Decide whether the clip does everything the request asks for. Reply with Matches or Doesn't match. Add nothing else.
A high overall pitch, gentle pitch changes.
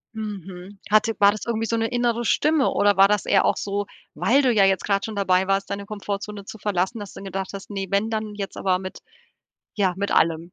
Matches